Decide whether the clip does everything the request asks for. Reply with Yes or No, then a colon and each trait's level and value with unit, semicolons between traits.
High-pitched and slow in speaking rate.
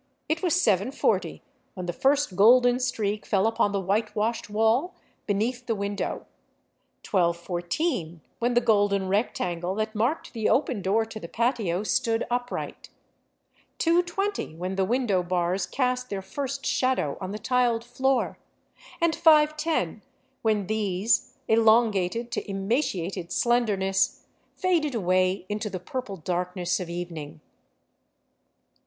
Yes: high, 215 Hz; slow, 130 wpm